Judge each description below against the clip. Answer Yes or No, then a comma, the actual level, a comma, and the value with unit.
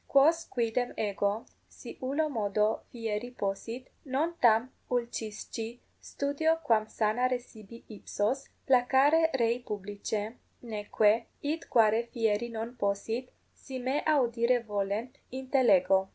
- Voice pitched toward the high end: Yes, high, 235 Hz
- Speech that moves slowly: Yes, slow, 110 wpm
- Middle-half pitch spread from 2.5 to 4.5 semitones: Yes, average, 3.3 semitones